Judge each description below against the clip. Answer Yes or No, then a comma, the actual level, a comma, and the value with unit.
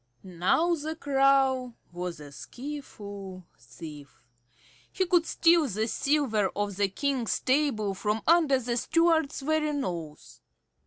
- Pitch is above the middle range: Yes, very high, 255 Hz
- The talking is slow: Yes, slow, 120 wpm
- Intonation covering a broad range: Yes, wide, 7.5 semitones